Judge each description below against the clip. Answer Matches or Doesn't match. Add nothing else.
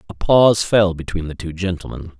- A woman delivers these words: Doesn't match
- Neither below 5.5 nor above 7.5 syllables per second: Matches